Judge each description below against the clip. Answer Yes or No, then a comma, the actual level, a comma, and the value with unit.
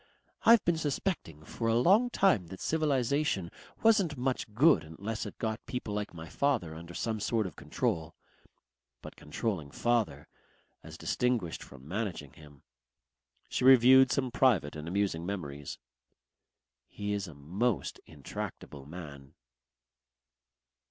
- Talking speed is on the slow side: Yes, slow, 130 wpm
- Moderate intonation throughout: No, wide, 8.2 semitones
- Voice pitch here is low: Yes, low, 105 Hz